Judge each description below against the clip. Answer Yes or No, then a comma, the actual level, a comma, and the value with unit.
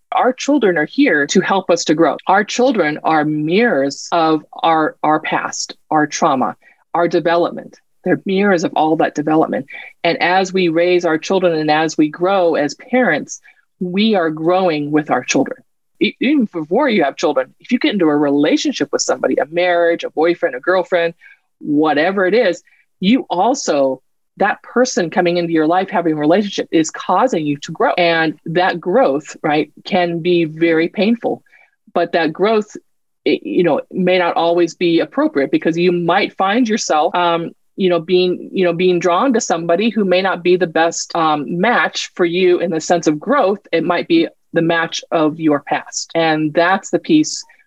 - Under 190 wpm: Yes, average, 180 wpm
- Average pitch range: Yes, average, 3.5 semitones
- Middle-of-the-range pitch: Yes, medium, 175 Hz